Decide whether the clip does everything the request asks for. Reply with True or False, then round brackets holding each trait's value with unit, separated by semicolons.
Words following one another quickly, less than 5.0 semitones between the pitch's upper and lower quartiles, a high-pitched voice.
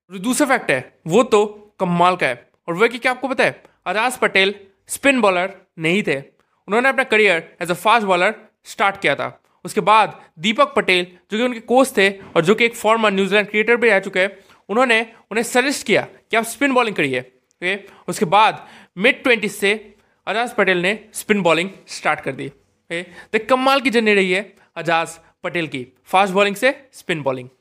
True (195 wpm; 4.3 semitones; 205 Hz)